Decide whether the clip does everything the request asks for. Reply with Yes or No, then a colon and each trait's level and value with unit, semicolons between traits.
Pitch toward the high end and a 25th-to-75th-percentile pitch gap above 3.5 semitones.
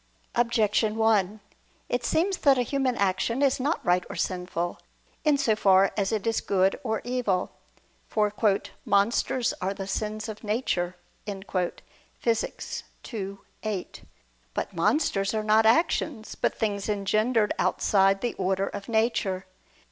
No: high, 215 Hz; average, 3.2 semitones